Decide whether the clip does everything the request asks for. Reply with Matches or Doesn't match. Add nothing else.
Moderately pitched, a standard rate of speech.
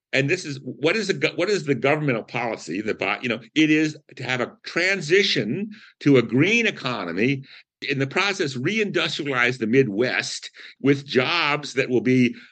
Matches